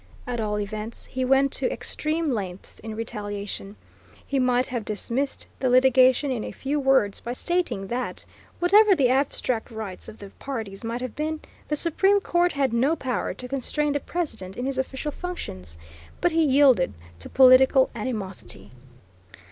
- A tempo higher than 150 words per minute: Yes, average, 165 wpm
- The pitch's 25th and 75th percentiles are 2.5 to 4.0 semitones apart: No, average, 4.6 semitones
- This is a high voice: Yes, very high, 255 Hz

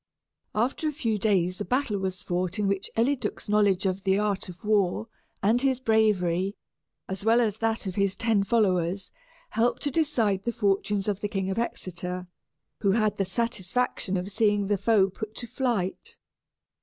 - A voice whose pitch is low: No, high, 205 Hz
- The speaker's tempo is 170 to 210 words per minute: Yes, average, 175 wpm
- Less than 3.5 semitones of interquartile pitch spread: Yes, average, 3.1 semitones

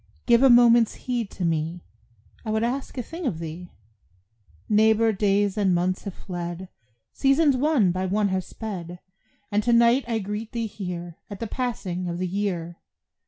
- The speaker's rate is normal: Yes, average, 170 wpm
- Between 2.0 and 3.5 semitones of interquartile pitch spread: No, average, 4.6 semitones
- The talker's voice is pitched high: Yes, high, 205 Hz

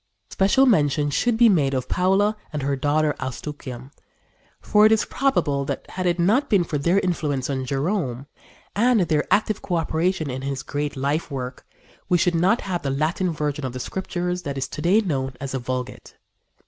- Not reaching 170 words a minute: No, average, 185 wpm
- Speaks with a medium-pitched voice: Yes, medium, 155 Hz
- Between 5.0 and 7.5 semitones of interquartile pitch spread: Yes, wide, 5.4 semitones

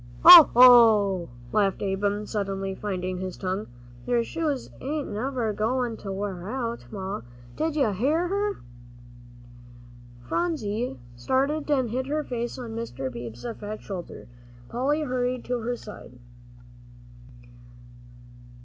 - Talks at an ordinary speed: No, slow, 120 wpm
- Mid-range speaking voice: No, high, 230 Hz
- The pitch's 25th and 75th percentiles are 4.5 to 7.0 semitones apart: Yes, average, 5.1 semitones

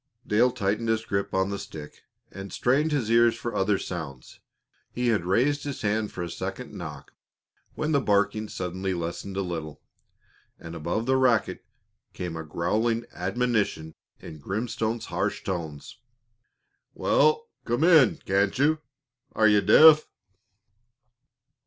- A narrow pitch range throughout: No, average, 5.1 semitones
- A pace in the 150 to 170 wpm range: No, average, 140 wpm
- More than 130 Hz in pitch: No, low, 105 Hz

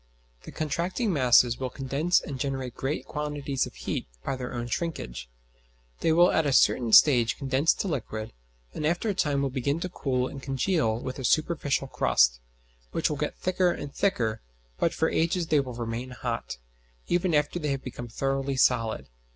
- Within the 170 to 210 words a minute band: Yes, average, 180 wpm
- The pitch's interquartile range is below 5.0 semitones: Yes, average, 4.1 semitones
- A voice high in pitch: No, low, 135 Hz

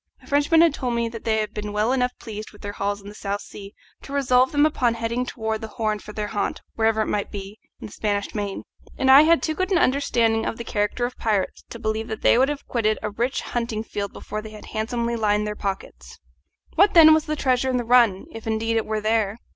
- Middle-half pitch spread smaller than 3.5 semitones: Yes, average, 3.0 semitones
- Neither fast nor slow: No, fast, 250 wpm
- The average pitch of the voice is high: Yes, high, 225 Hz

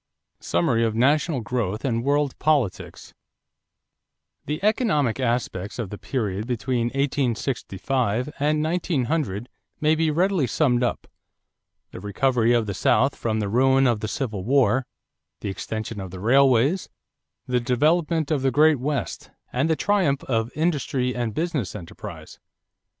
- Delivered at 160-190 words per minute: No, average, 140 wpm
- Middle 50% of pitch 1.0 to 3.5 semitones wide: No, average, 4.7 semitones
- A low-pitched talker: Yes, low, 125 Hz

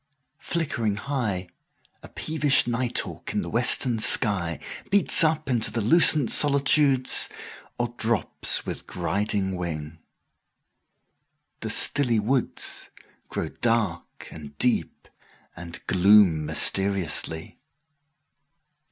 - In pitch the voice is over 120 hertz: No, low, 110 Hz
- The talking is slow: Yes, slow, 85 wpm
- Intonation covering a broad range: Yes, wide, 6.8 semitones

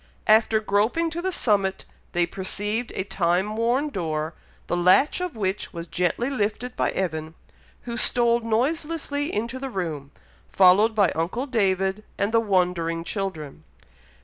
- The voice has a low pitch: No, high, 205 Hz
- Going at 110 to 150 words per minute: Yes, average, 145 wpm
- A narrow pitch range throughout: No, average, 4.8 semitones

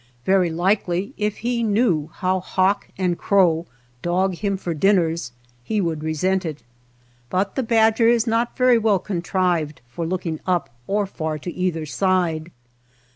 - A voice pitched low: No, medium, 185 Hz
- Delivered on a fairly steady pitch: No, average, 3.7 semitones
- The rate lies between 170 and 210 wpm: No, average, 150 wpm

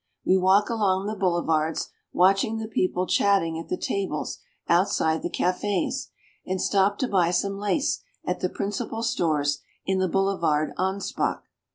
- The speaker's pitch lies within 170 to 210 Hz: Yes, high, 190 Hz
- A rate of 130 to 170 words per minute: Yes, average, 155 wpm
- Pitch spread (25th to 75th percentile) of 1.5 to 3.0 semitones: Yes, average, 2.7 semitones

